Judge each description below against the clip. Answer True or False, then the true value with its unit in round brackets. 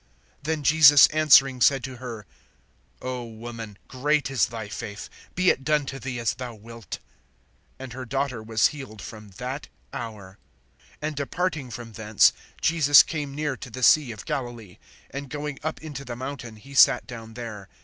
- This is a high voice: False (130 Hz)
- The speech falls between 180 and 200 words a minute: False (170 wpm)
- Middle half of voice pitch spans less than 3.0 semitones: False (3.8 semitones)